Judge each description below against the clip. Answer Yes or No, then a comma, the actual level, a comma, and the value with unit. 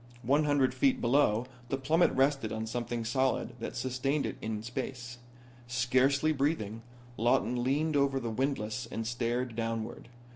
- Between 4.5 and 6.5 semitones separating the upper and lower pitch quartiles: No, average, 3.0 semitones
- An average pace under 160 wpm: Yes, average, 150 wpm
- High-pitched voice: No, low, 125 Hz